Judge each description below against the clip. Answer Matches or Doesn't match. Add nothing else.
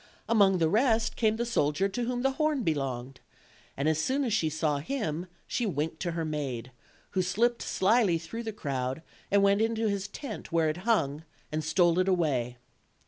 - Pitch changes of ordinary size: Doesn't match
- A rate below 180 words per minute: Doesn't match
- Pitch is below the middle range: Doesn't match